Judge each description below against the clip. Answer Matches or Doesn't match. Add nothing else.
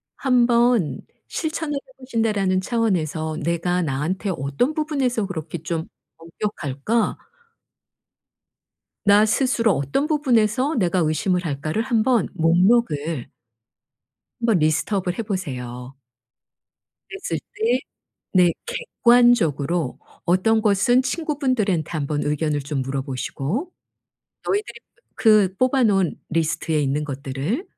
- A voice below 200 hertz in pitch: Matches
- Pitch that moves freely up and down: Matches